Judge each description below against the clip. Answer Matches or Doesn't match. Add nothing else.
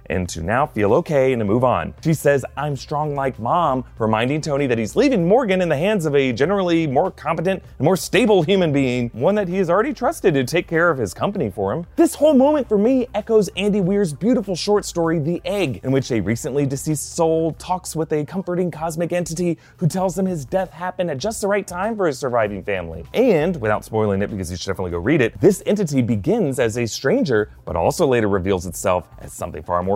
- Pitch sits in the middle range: Matches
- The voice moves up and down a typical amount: Doesn't match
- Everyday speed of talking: Doesn't match